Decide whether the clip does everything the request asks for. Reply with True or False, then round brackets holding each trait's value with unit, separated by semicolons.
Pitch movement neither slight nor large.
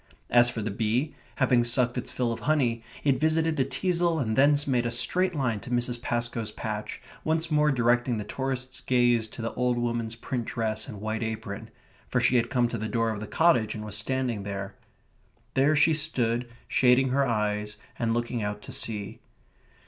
True (3.1 semitones)